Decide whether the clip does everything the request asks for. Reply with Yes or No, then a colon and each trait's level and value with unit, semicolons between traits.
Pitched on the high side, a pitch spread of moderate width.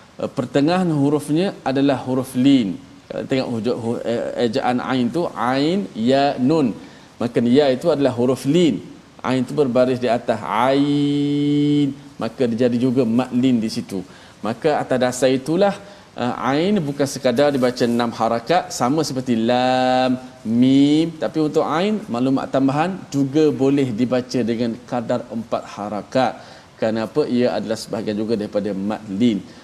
No: low, 130 Hz; average, 3.0 semitones